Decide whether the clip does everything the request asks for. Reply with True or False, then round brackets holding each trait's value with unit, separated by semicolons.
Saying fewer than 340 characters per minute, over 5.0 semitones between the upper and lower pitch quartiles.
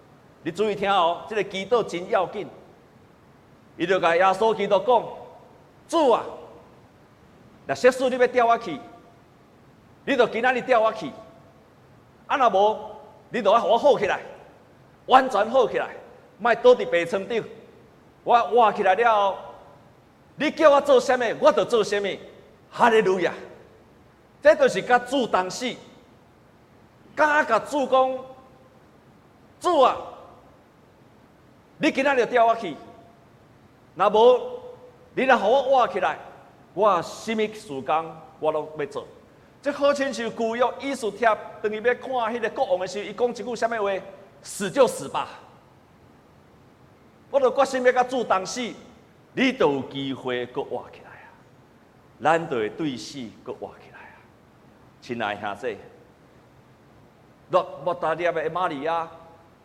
True (190 characters per minute; 5.6 semitones)